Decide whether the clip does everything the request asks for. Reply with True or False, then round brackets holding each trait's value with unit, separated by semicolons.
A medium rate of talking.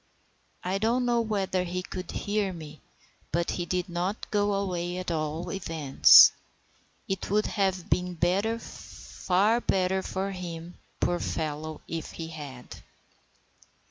False (130 wpm)